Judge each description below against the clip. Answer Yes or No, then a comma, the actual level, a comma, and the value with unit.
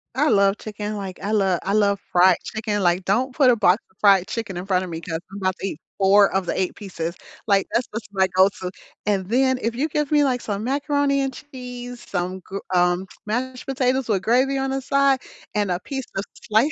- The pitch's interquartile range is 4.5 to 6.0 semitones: Yes, average, 5.3 semitones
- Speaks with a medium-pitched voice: No, high, 210 Hz